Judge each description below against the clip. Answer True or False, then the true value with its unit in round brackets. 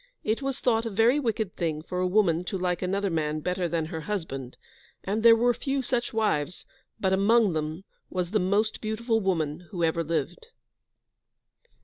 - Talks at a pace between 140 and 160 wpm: False (175 wpm)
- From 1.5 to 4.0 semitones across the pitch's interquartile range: False (5.0 semitones)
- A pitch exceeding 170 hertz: True (190 Hz)